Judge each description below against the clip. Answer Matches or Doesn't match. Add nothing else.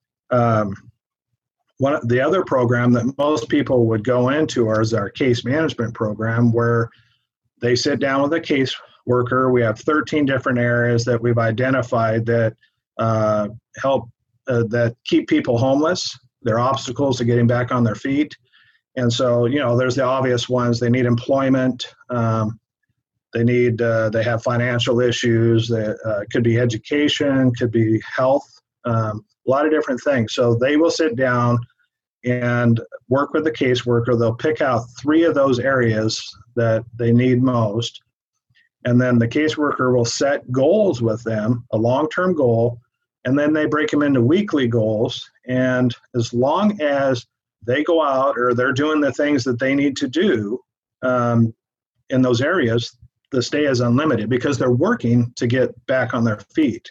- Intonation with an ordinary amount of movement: Doesn't match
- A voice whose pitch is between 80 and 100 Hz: Doesn't match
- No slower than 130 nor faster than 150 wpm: Doesn't match